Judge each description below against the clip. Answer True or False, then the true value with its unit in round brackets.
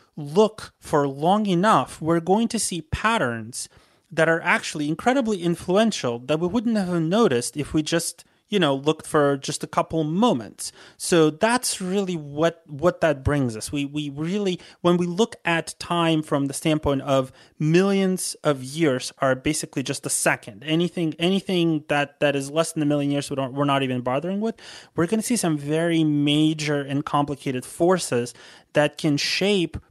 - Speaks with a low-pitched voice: False (160 Hz)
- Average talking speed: True (175 wpm)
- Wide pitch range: False (3.8 semitones)